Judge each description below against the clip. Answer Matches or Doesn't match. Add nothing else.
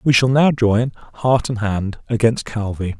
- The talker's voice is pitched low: Matches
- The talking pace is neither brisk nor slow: Matches